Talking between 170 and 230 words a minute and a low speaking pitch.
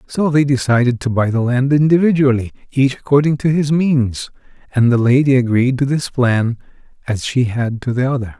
Yes: average, 185 wpm; low, 130 Hz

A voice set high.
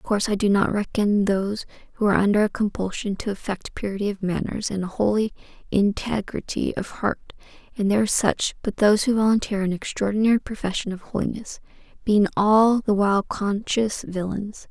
Yes: high, 205 Hz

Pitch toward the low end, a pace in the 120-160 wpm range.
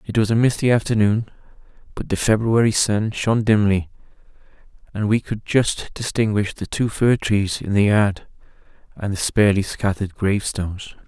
Yes: low, 105 Hz; average, 150 wpm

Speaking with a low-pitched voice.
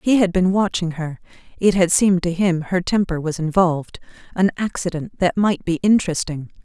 No: medium, 180 Hz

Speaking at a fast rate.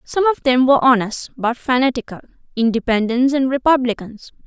No: slow, 135 wpm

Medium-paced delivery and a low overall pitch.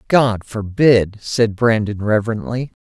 No: slow, 105 wpm; low, 110 Hz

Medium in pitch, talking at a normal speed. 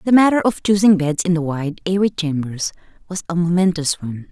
Yes: medium, 175 Hz; average, 195 wpm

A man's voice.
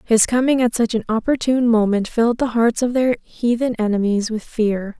No: female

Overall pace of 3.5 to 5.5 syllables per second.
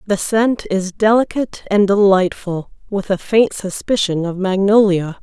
Yes: 4.5 syllables/s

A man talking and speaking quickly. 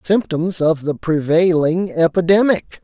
No: male; slow, 105 wpm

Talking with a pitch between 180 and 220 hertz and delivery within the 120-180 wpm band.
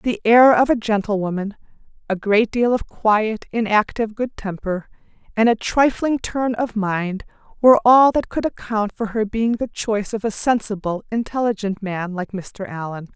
Yes: high, 215 Hz; average, 170 wpm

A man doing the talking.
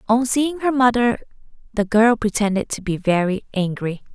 No: female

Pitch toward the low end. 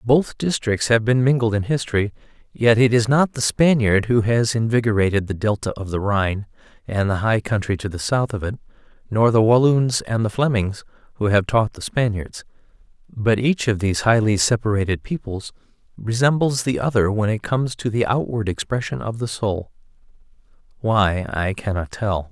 Yes: low, 110 Hz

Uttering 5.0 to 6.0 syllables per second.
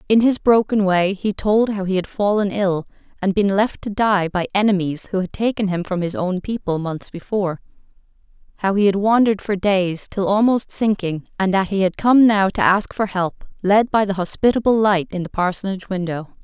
Yes: 5.2 syllables/s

